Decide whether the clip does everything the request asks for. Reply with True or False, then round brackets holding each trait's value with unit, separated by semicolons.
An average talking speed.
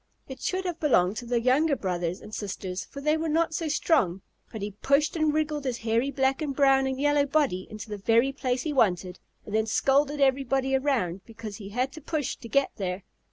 False (215 wpm)